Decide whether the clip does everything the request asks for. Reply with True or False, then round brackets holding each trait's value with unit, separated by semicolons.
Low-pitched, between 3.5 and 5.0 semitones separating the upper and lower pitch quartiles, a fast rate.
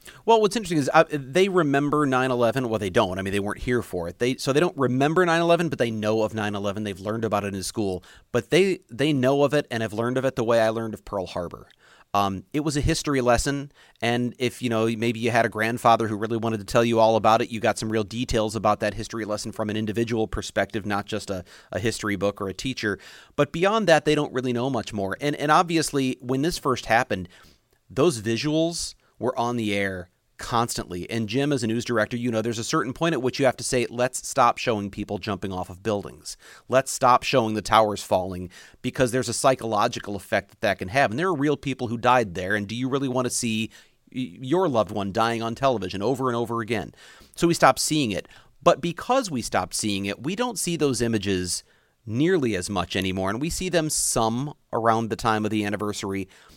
True (115 Hz; 4.1 semitones; 230 wpm)